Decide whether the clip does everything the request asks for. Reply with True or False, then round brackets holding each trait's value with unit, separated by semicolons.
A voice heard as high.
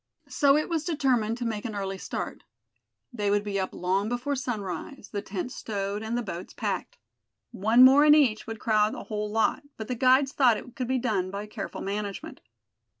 True (220 Hz)